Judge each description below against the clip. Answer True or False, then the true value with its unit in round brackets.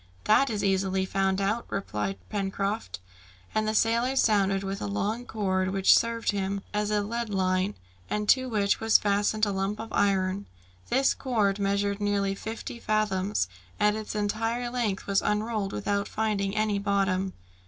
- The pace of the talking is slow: False (160 wpm)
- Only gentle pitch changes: True (1.8 semitones)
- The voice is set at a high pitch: True (205 Hz)